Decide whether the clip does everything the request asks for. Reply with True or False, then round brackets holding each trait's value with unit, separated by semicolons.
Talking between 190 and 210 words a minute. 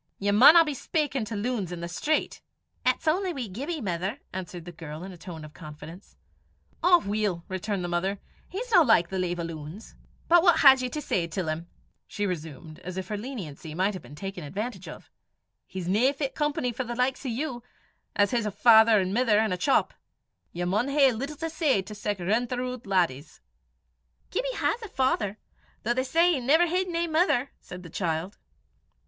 True (200 wpm)